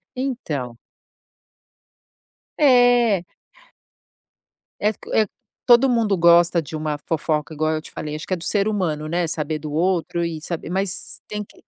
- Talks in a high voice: No, medium, 170 Hz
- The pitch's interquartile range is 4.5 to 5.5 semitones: Yes, average, 5.2 semitones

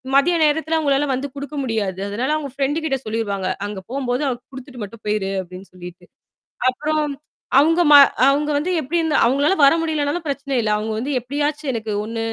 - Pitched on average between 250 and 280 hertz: Yes, very high, 270 Hz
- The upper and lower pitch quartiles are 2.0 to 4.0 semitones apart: No, average, 5.2 semitones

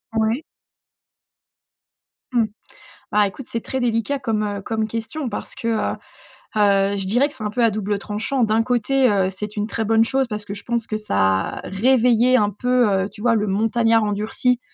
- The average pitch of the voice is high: Yes, high, 220 Hz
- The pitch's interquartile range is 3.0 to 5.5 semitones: No, narrow, 2.6 semitones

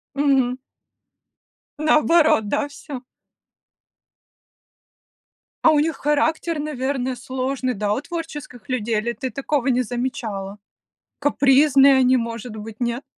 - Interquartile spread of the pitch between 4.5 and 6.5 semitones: No, average, 3.3 semitones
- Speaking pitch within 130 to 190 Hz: No, very high, 260 Hz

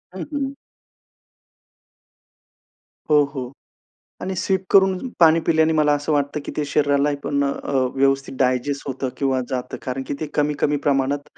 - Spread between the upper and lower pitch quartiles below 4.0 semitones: Yes, narrow, 2.4 semitones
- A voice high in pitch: No, medium, 145 Hz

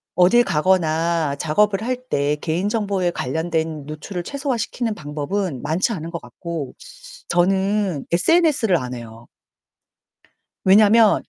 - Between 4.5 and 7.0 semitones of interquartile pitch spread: Yes, average, 5.2 semitones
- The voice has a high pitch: No, medium, 175 Hz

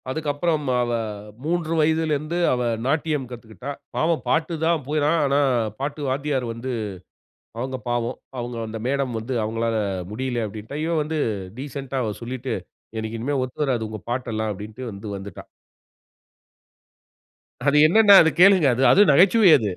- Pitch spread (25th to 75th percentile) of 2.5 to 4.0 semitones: No, average, 4.8 semitones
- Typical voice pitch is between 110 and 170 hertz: Yes, low, 135 Hz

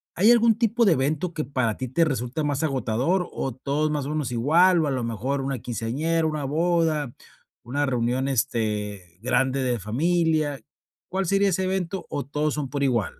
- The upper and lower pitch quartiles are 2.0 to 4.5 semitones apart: No, average, 4.9 semitones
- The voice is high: No, medium, 140 Hz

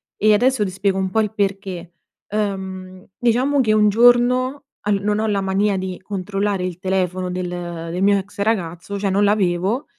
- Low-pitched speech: No, high, 200 Hz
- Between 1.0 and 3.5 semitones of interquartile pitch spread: Yes, narrow, 2.4 semitones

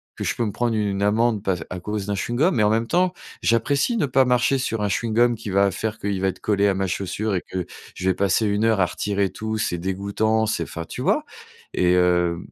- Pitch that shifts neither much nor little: Yes, average, 3.0 semitones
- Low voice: Yes, low, 105 Hz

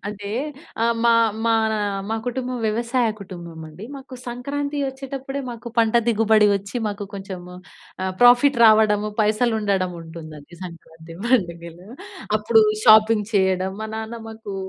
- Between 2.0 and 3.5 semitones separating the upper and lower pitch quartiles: No, average, 4.0 semitones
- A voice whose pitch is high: Yes, high, 215 Hz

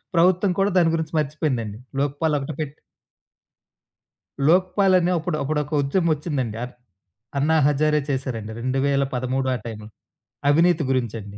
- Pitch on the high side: No, medium, 145 Hz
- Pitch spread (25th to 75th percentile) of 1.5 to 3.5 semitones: No, average, 4.0 semitones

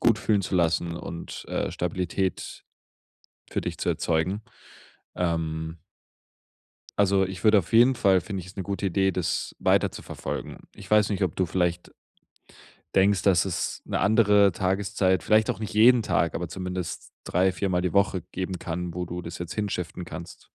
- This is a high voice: No, very low, 95 Hz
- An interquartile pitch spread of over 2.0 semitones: Yes, narrow, 2.5 semitones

